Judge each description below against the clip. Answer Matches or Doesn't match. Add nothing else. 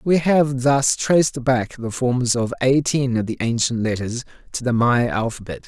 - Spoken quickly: Doesn't match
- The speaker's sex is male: Matches